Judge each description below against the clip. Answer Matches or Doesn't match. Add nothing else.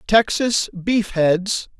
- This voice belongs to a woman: Doesn't match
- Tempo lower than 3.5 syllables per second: Matches